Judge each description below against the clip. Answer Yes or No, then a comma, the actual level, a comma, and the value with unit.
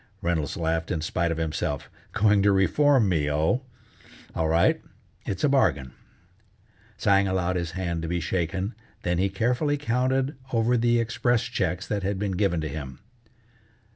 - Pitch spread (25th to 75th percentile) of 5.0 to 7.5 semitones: Yes, wide, 5.6 semitones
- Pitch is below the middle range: Yes, very low, 95 Hz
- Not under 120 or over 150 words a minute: No, average, 160 wpm